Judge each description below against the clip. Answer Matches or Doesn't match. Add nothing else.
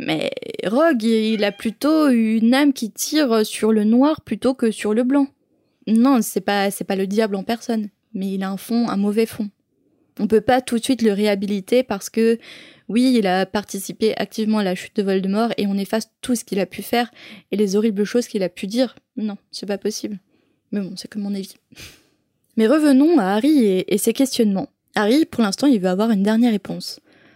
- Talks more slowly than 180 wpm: Doesn't match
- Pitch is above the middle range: Matches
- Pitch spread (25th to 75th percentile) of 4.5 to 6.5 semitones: Doesn't match